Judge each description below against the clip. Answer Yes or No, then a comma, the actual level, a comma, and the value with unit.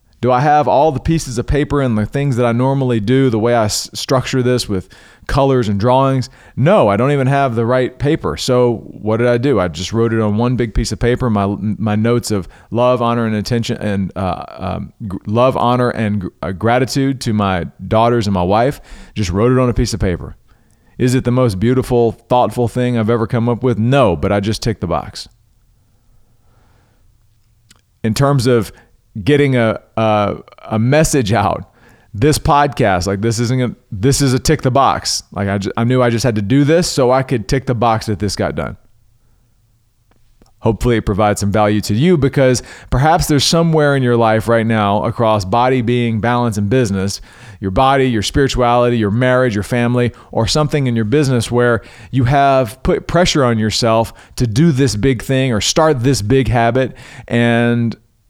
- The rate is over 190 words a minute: Yes, average, 200 wpm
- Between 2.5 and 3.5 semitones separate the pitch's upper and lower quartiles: Yes, average, 3.2 semitones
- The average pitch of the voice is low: Yes, low, 120 Hz